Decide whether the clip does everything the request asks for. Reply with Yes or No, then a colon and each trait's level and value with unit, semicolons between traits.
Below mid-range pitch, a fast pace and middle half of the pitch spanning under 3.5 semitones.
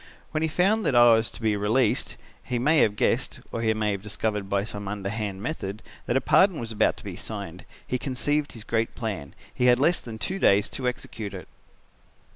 No: low, 115 Hz; fast, 215 wpm; average, 4.1 semitones